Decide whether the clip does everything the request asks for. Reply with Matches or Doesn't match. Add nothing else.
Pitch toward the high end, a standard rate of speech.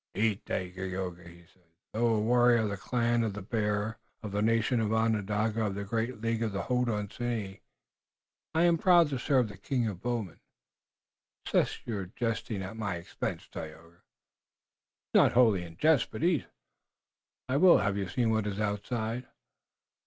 Doesn't match